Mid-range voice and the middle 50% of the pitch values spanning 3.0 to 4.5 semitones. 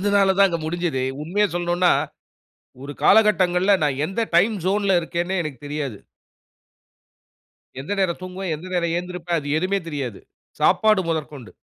Yes: medium, 175 Hz; average, 3.8 semitones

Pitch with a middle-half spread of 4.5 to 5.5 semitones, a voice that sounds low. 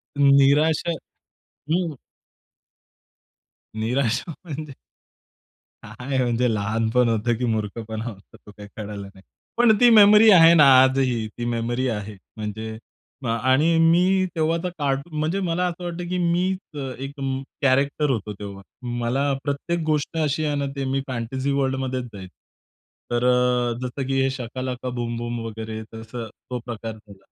Yes: average, 4.9 semitones; low, 130 Hz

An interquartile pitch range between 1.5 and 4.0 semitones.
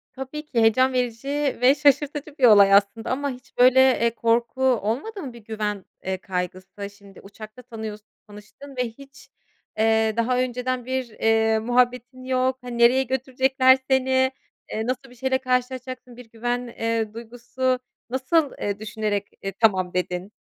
Yes: average, 3.0 semitones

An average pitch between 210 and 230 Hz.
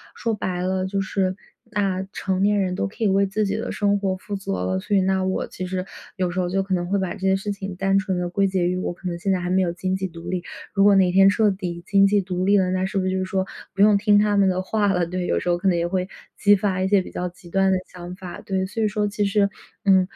No: high, 190 Hz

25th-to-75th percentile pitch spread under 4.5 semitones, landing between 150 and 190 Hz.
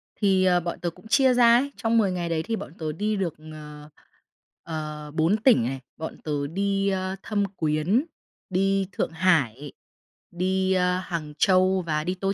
Yes: average, 4.1 semitones; medium, 185 Hz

